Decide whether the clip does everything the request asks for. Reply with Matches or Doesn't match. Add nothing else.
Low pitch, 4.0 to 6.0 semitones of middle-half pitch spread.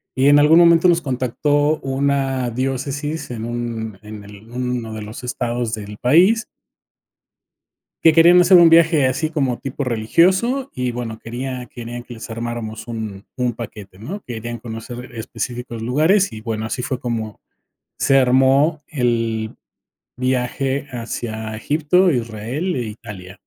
Matches